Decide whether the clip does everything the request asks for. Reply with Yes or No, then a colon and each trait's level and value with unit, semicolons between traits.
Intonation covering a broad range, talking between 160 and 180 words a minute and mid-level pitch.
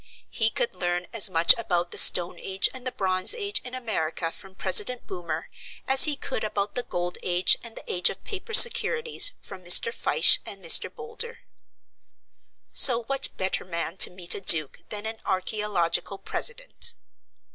No: wide, 6.8 semitones; average, 170 wpm; high, 200 Hz